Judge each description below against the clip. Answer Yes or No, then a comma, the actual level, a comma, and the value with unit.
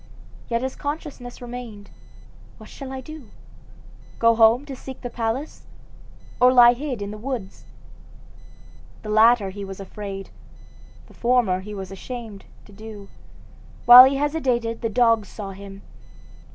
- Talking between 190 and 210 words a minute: No, average, 140 wpm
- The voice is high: Yes, high, 230 Hz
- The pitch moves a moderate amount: Yes, average, 3.7 semitones